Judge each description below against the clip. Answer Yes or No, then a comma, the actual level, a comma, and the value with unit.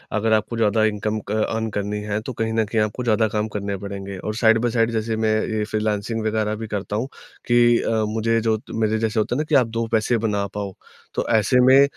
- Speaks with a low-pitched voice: Yes, low, 110 Hz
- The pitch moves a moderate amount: No, narrow, 1.4 semitones